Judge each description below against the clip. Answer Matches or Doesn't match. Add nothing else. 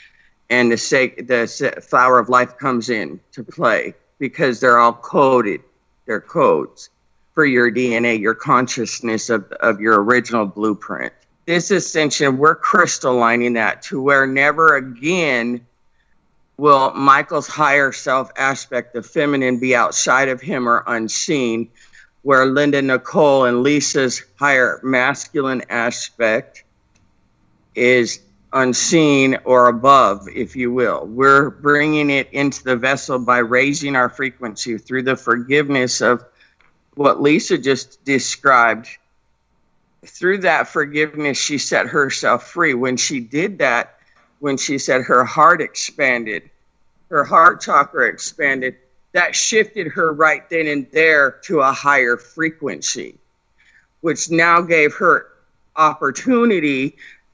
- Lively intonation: Doesn't match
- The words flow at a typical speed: Doesn't match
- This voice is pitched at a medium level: Doesn't match